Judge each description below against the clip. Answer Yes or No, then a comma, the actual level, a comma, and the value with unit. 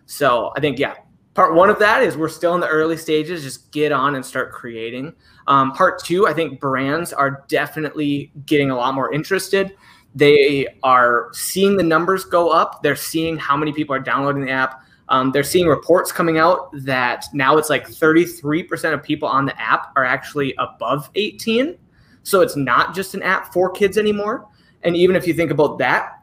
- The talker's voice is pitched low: No, medium, 150 Hz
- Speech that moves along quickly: No, average, 195 wpm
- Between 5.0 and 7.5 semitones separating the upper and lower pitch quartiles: No, average, 4.1 semitones